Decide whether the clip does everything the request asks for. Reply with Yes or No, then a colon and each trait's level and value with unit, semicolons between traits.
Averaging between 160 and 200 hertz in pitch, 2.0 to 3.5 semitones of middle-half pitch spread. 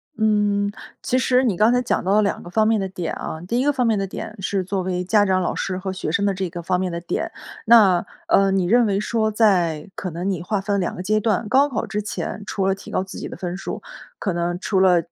Yes: high, 195 Hz; average, 2.8 semitones